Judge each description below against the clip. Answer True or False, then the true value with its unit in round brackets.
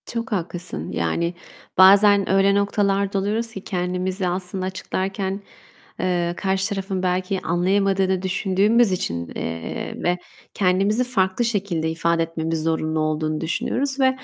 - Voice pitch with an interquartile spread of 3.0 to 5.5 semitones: False (2.5 semitones)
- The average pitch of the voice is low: False (190 Hz)